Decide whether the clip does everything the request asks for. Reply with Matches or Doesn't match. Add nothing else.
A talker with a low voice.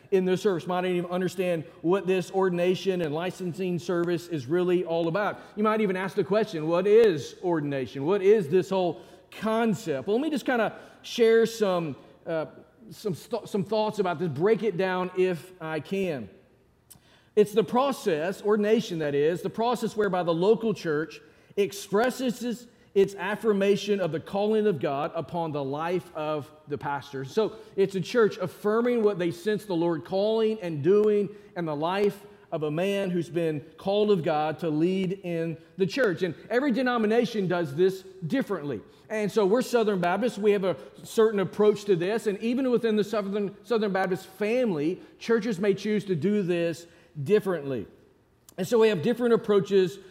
Doesn't match